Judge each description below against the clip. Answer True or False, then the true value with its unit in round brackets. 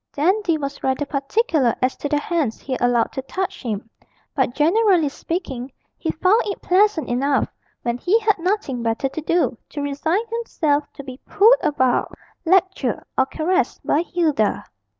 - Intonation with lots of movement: True (6.0 semitones)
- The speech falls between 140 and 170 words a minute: True (160 wpm)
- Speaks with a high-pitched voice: True (300 Hz)